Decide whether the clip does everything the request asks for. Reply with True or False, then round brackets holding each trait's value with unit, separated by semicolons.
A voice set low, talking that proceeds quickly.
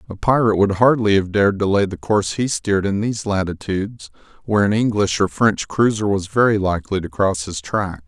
True (100 Hz; 210 wpm)